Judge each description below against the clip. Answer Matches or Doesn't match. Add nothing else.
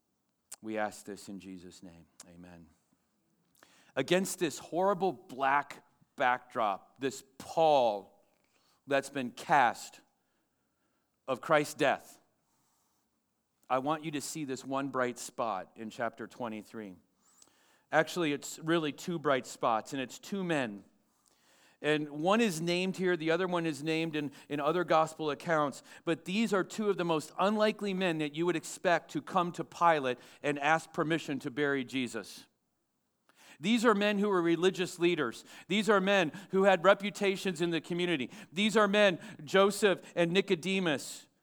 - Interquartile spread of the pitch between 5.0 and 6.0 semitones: Matches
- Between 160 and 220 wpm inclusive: Doesn't match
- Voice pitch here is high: Doesn't match